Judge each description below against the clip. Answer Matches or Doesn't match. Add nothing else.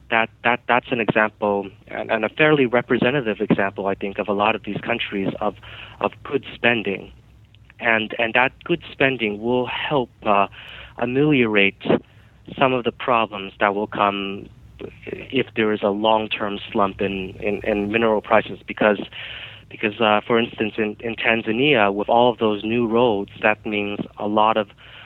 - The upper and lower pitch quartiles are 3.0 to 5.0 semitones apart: Doesn't match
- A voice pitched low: Matches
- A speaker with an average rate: Matches